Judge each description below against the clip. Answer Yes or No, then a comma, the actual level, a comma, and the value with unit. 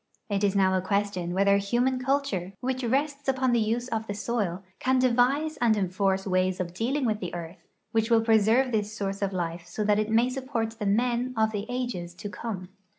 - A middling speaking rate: No, fast, 210 wpm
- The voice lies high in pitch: Yes, high, 215 Hz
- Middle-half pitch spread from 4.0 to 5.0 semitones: Yes, average, 4.3 semitones